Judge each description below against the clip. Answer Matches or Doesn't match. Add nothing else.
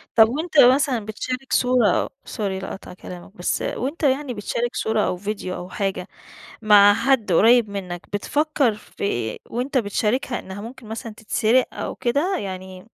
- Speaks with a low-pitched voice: Doesn't match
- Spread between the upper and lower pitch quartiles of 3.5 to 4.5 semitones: Matches